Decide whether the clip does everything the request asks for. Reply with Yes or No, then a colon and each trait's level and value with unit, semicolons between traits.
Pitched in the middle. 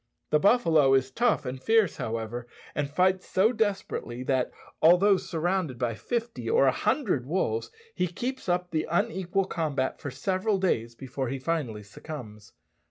Yes: medium, 160 Hz